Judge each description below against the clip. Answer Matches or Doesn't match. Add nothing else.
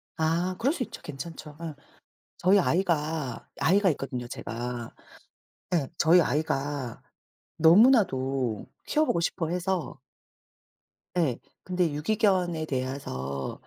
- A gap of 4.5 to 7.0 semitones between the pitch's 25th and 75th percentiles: Matches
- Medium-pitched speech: Matches